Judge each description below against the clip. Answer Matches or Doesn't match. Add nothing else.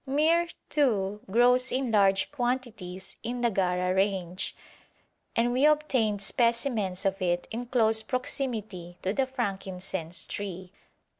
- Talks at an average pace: Doesn't match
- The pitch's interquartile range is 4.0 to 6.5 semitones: Matches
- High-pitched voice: Matches